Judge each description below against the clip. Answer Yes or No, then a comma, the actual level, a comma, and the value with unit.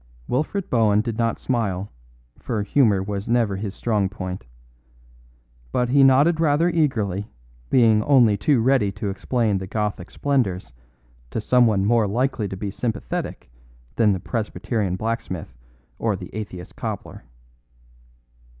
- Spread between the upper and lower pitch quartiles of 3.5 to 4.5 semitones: Yes, average, 4.0 semitones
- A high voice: No, low, 110 Hz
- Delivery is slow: Yes, slow, 130 wpm